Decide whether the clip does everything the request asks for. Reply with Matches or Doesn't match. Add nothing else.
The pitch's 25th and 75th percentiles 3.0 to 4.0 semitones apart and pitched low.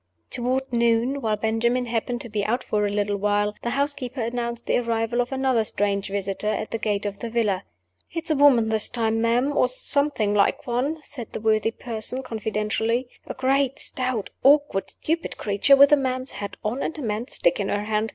Doesn't match